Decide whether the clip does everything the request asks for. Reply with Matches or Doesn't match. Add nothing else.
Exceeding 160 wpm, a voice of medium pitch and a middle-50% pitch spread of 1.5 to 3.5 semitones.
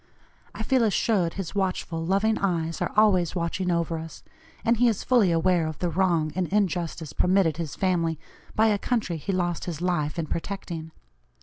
Matches